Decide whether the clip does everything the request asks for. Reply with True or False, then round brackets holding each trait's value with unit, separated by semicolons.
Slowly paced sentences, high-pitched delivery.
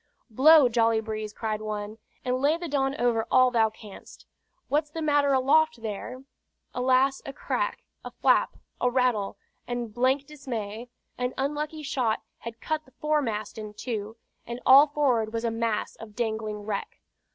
False (160 wpm; 245 Hz)